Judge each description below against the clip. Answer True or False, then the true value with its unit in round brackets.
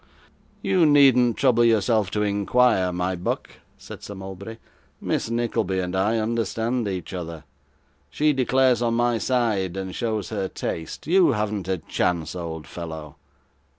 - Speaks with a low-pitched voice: True (105 Hz)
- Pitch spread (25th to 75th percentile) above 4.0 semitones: True (4.6 semitones)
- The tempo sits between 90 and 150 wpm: True (145 wpm)